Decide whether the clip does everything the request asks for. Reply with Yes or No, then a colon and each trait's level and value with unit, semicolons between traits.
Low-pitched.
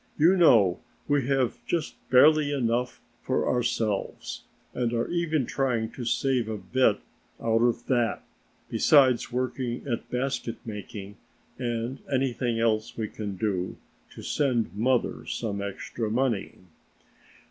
Yes: low, 120 Hz